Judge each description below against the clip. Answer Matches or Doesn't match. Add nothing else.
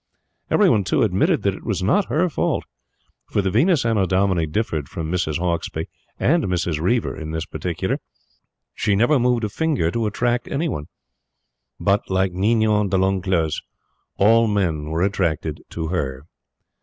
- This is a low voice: Matches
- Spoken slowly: Doesn't match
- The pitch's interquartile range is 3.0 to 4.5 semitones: Doesn't match